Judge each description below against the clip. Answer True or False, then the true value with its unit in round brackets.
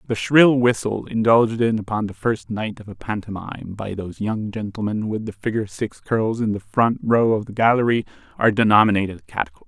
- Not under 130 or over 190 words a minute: False (200 wpm)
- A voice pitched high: False (110 Hz)